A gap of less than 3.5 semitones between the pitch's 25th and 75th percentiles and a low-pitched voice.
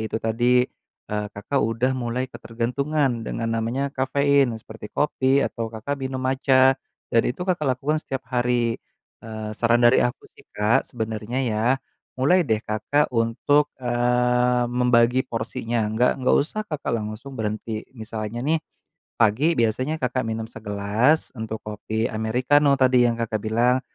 Yes: average, 2.9 semitones; low, 120 Hz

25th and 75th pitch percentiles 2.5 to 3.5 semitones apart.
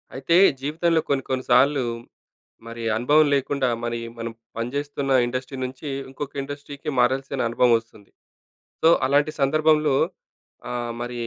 Yes: average, 2.8 semitones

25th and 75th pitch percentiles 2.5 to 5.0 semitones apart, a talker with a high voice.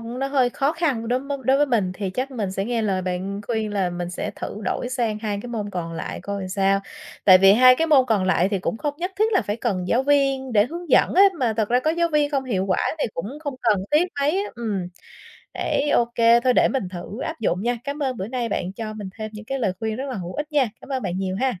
No: wide, 5.5 semitones; high, 230 Hz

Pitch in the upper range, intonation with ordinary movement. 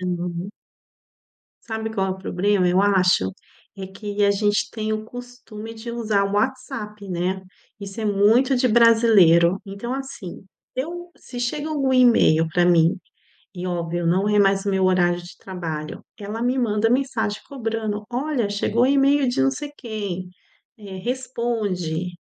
Yes: high, 210 Hz; average, 4.5 semitones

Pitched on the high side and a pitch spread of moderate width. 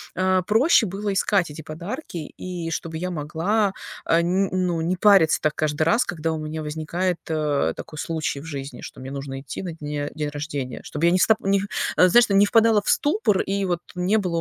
No: medium, 170 Hz; average, 4.1 semitones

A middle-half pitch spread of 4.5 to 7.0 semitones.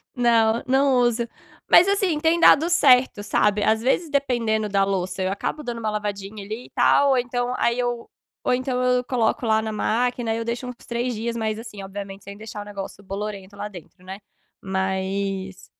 No: average, 3.7 semitones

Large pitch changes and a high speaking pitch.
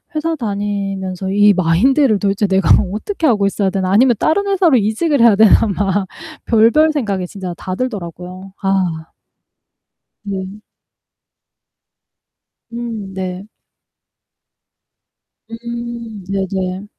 No: average, 3.7 semitones; high, 205 Hz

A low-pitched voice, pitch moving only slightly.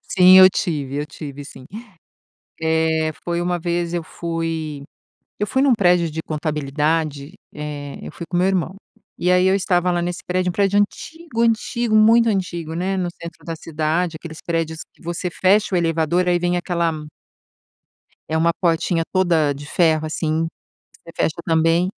No: medium, 170 Hz; narrow, 2.3 semitones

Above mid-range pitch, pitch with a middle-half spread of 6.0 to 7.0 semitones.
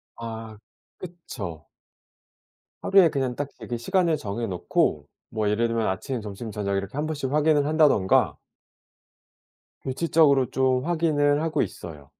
No: low, 130 Hz; wide, 6.4 semitones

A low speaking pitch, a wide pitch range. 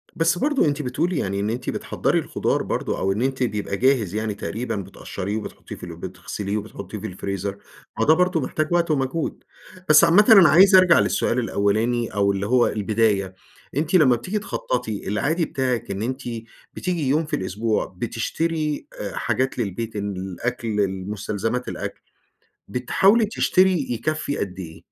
Yes: low, 120 Hz; wide, 7.3 semitones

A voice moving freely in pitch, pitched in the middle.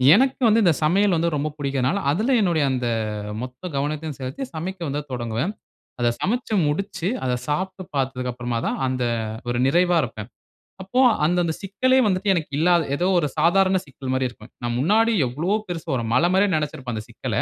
Yes: wide, 6.7 semitones; medium, 155 Hz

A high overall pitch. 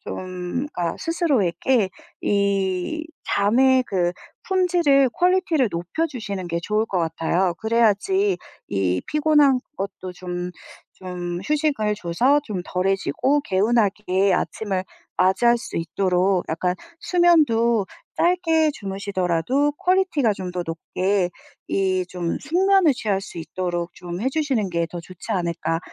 Yes: high, 200 Hz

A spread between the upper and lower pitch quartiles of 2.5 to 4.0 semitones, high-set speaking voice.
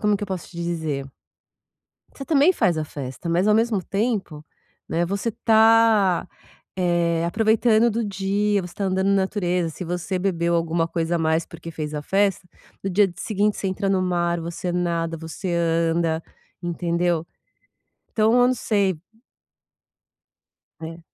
No: average, 3.5 semitones; medium, 180 Hz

